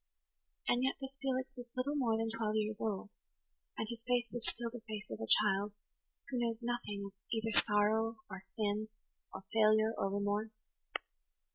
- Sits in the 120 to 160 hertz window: No, high, 220 Hz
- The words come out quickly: No, average, 170 wpm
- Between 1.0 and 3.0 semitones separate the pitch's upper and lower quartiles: Yes, narrow, 2.4 semitones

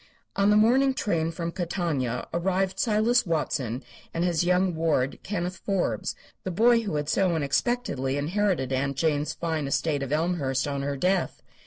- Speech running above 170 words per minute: No, average, 160 wpm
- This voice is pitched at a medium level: Yes, medium, 170 Hz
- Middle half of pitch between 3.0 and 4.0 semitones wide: No, average, 5.2 semitones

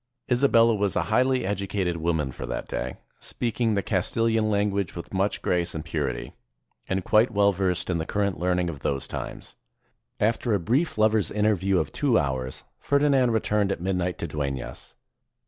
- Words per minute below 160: No, average, 165 wpm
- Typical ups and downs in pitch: Yes, average, 4.5 semitones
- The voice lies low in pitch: Yes, low, 100 Hz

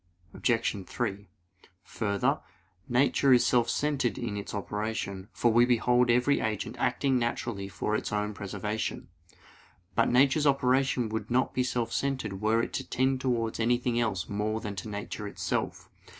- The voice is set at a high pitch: No, low, 115 Hz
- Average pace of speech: Yes, average, 150 wpm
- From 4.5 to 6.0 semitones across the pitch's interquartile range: No, average, 3.2 semitones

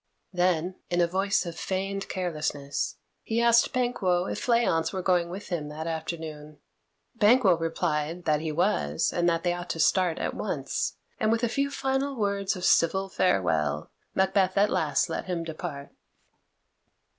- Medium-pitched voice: Yes, medium, 175 Hz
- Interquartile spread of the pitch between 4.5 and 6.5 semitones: No, average, 3.6 semitones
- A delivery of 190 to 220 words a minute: No, average, 160 wpm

